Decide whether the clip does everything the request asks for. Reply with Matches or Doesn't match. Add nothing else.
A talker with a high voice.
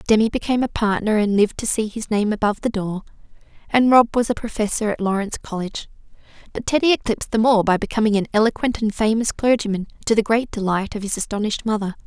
Matches